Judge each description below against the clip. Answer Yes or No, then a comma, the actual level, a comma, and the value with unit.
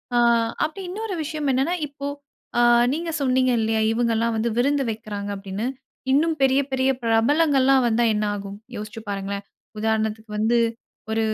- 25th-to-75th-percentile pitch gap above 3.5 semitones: Yes, average, 4.2 semitones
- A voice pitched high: Yes, high, 235 Hz